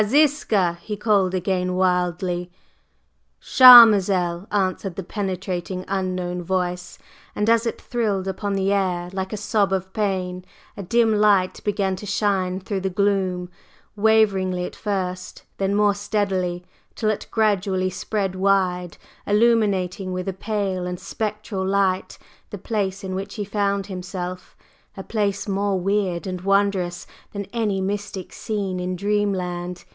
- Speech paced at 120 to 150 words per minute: Yes, average, 140 wpm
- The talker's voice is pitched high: Yes, high, 195 Hz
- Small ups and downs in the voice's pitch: Yes, narrow, 2.0 semitones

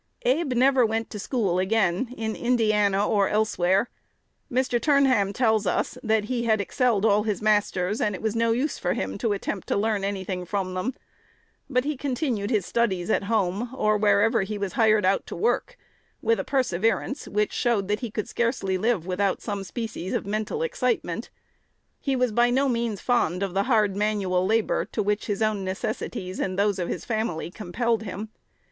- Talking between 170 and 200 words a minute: Yes, average, 190 wpm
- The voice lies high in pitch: Yes, high, 215 Hz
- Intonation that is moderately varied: Yes, average, 3.3 semitones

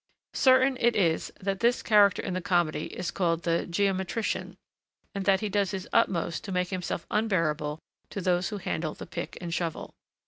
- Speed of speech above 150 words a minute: Yes, average, 180 wpm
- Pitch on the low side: No, medium, 185 Hz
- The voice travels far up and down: No, average, 3.1 semitones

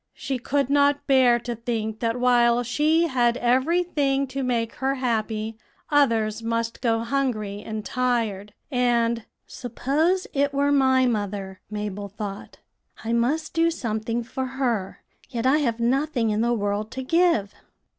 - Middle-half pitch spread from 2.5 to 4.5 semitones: Yes, average, 3.6 semitones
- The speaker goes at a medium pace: Yes, average, 150 wpm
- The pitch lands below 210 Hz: No, high, 240 Hz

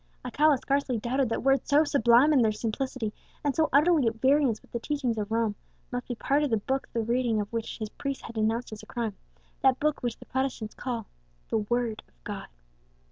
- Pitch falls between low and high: No, high, 245 Hz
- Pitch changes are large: No, average, 3.6 semitones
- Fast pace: Yes, fast, 215 wpm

